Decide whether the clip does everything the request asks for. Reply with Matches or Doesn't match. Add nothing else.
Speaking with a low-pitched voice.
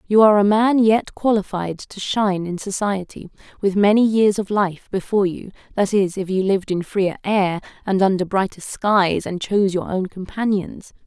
Doesn't match